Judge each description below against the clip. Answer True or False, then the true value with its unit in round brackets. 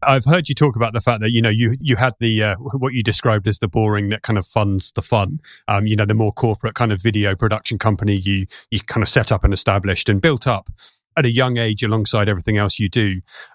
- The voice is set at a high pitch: False (110 Hz)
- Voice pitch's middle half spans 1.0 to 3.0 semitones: True (2.4 semitones)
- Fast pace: True (255 wpm)